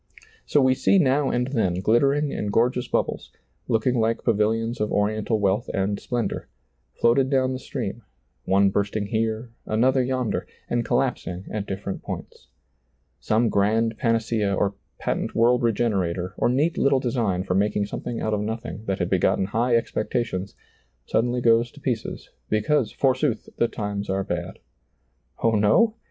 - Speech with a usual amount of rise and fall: Yes, average, 3.3 semitones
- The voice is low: Yes, low, 115 Hz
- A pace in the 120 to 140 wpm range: No, average, 155 wpm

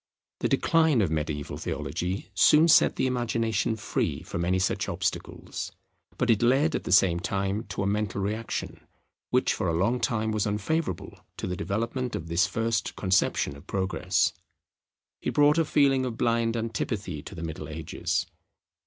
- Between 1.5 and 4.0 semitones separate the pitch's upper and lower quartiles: No, average, 4.5 semitones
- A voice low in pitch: Yes, low, 105 Hz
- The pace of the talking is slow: No, average, 165 wpm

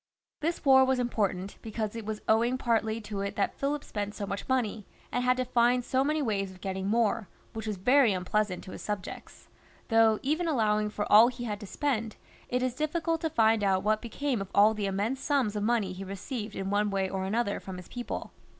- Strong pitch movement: No, average, 3.7 semitones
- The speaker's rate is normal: No, fast, 220 wpm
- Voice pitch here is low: No, high, 220 Hz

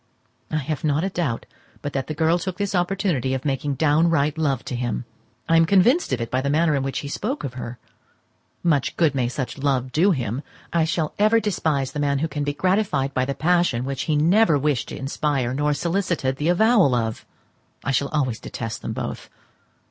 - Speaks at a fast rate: Yes, fast, 210 wpm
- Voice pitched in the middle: Yes, medium, 145 Hz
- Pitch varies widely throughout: No, average, 4.2 semitones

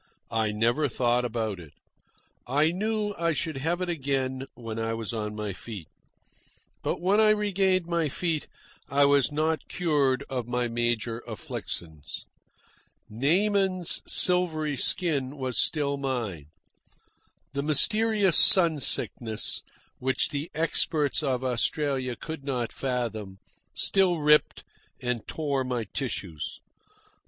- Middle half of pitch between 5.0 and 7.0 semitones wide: Yes, wide, 5.6 semitones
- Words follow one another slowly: Yes, slow, 125 wpm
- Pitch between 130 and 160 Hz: Yes, medium, 140 Hz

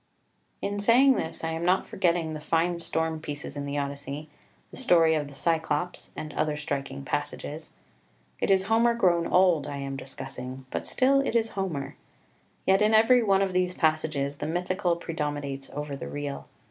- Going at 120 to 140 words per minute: No, average, 180 wpm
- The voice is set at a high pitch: No, medium, 160 Hz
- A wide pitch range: No, average, 4.6 semitones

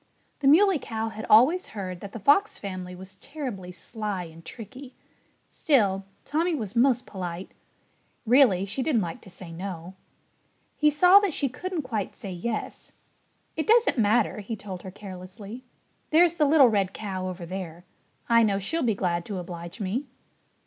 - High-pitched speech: Yes, high, 215 Hz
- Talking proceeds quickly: No, average, 165 wpm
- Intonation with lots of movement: Yes, wide, 6.6 semitones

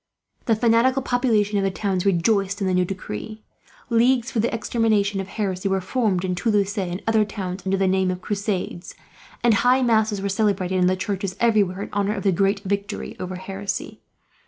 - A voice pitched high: Yes, high, 200 Hz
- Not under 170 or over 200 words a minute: Yes, average, 190 wpm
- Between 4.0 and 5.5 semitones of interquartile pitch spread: No, average, 2.7 semitones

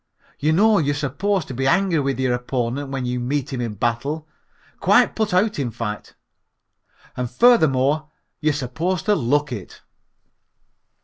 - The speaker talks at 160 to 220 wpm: No, average, 145 wpm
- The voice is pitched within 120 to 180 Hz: Yes, medium, 140 Hz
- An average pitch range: Yes, average, 4.5 semitones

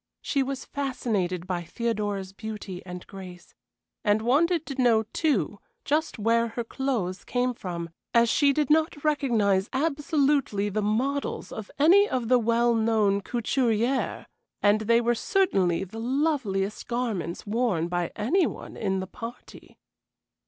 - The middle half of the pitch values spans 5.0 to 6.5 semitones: Yes, wide, 5.4 semitones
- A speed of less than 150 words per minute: Yes, average, 140 wpm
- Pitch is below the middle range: No, high, 230 Hz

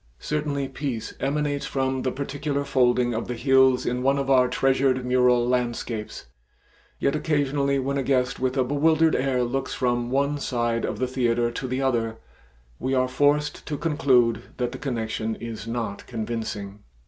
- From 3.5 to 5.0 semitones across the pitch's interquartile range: No, narrow, 2.4 semitones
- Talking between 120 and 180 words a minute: Yes, average, 165 wpm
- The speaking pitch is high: No, low, 130 Hz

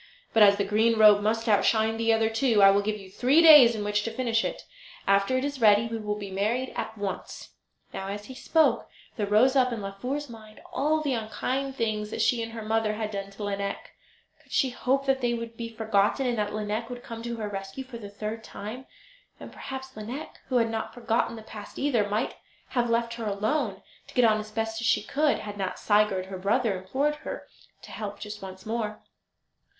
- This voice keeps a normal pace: No, fast, 220 wpm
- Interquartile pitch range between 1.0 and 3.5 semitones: Yes, average, 2.8 semitones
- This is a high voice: Yes, high, 225 Hz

